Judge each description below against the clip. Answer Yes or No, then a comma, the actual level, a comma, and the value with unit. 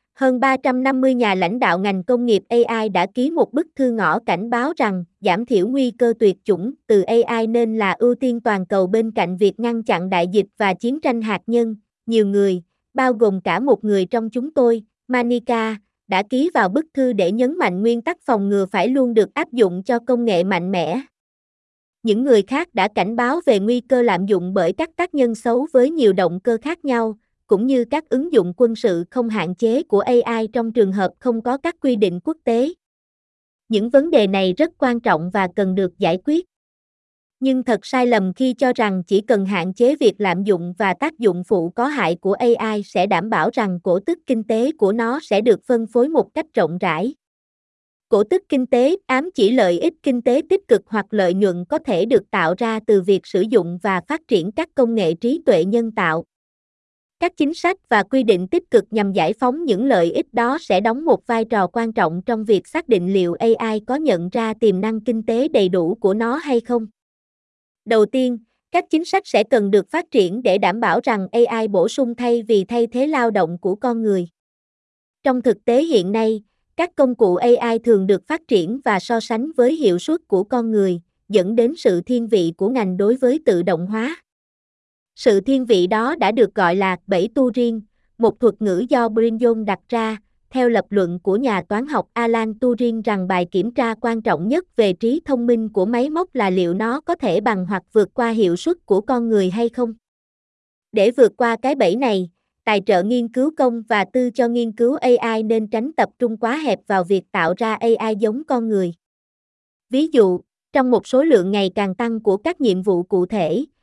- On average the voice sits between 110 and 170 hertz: No, high, 230 Hz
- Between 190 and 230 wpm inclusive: Yes, average, 215 wpm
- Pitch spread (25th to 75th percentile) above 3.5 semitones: Yes, average, 4.1 semitones